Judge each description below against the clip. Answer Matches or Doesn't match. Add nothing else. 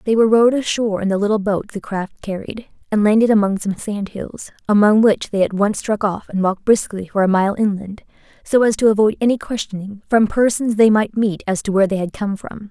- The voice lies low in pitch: Doesn't match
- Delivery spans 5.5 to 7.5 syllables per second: Matches